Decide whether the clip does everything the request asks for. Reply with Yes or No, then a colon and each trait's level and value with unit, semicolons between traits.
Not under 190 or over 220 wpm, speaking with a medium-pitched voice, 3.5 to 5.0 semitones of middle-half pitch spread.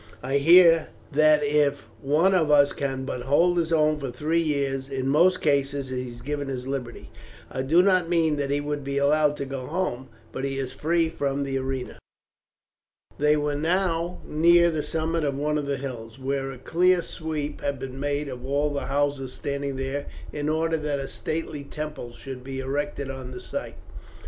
No: average, 195 wpm; medium, 145 Hz; narrow, 2.5 semitones